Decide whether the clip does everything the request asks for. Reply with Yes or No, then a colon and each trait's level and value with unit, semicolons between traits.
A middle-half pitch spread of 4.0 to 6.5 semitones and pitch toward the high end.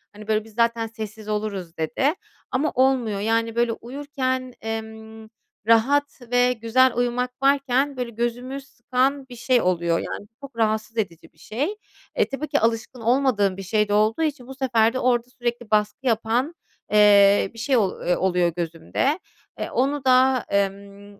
No: average, 3.3 semitones; high, 230 Hz